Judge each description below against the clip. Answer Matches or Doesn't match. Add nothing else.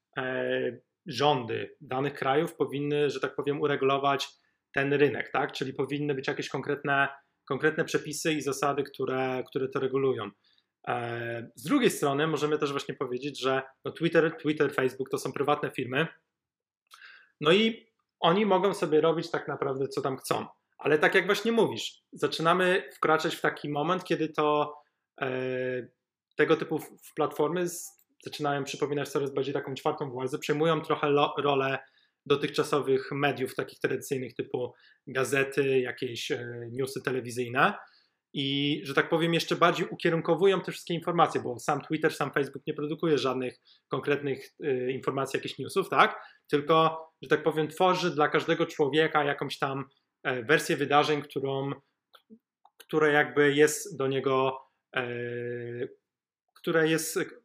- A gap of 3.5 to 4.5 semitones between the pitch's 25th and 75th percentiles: Doesn't match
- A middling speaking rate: Matches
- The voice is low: Doesn't match